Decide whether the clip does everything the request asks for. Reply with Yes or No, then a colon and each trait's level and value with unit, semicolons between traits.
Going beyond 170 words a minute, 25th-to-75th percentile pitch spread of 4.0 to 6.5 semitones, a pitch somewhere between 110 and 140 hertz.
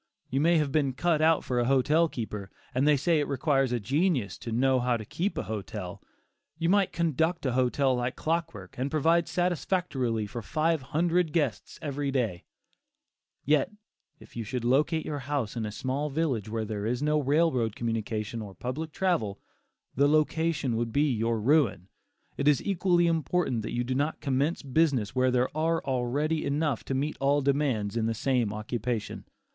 Yes: average, 180 wpm; average, 4.8 semitones; low, 135 Hz